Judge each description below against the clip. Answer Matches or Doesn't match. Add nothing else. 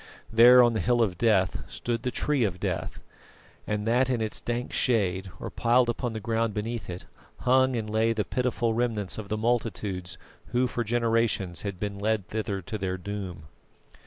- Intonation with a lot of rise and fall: Doesn't match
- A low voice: Matches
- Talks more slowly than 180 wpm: Doesn't match